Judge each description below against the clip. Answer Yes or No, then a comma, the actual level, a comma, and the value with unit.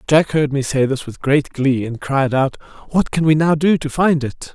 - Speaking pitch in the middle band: Yes, medium, 145 Hz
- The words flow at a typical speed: No, fast, 250 wpm